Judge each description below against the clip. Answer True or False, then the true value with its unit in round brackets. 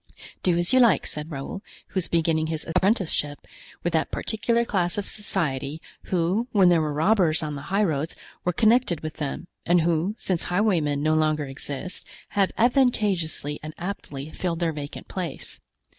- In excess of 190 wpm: False (165 wpm)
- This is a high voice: False (170 Hz)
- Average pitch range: True (4.2 semitones)